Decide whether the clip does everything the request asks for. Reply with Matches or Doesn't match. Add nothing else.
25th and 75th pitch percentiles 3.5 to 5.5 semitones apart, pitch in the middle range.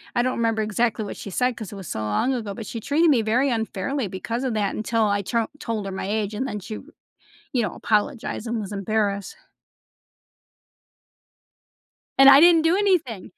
Doesn't match